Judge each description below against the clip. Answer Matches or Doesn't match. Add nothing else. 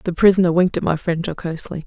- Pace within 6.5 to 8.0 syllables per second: Matches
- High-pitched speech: Doesn't match